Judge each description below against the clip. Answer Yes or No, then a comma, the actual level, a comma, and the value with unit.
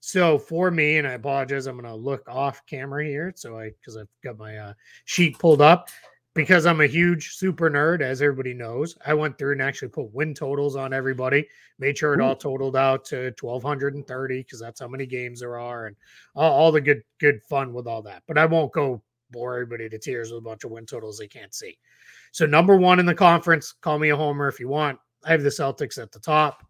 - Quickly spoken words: Yes, fast, 235 wpm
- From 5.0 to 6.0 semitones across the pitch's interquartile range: No, average, 3.7 semitones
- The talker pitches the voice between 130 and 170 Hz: Yes, medium, 140 Hz